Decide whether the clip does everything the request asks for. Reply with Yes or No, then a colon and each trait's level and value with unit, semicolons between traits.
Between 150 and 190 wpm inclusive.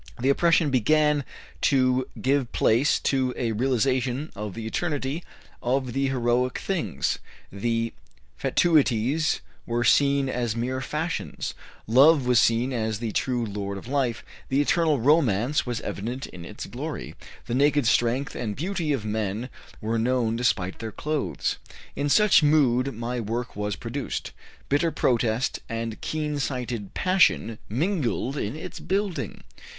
No: average, 140 wpm